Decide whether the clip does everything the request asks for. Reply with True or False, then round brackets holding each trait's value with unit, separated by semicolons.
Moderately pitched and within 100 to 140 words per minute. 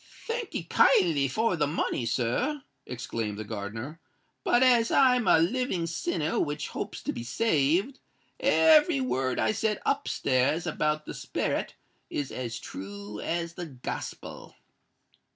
True (155 Hz; 135 wpm)